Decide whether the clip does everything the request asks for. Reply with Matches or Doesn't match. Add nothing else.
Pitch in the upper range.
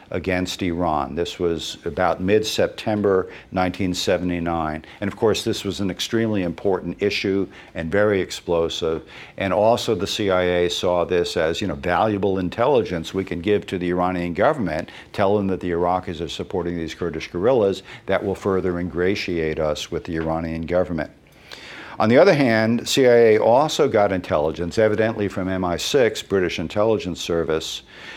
Doesn't match